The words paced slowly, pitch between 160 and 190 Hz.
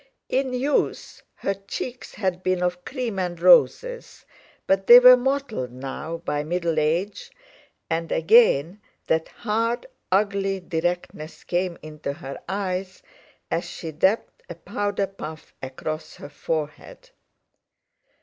Yes: slow, 120 wpm; medium, 185 Hz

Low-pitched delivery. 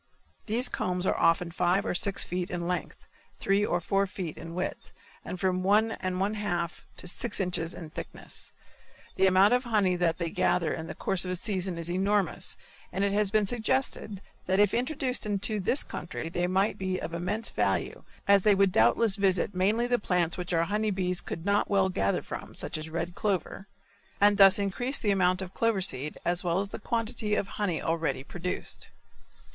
No: high, 190 Hz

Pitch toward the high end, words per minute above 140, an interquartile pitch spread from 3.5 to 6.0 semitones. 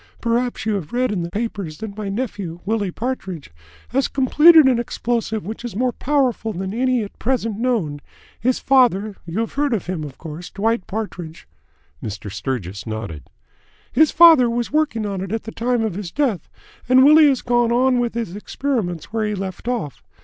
Yes: high, 225 Hz; average, 185 wpm; average, 5.2 semitones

